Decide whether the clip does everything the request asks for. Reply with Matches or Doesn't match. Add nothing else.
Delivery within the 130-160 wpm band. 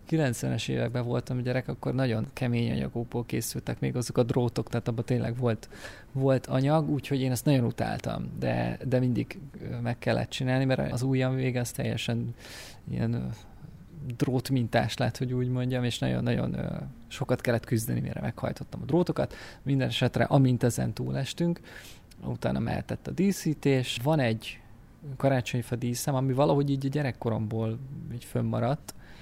Matches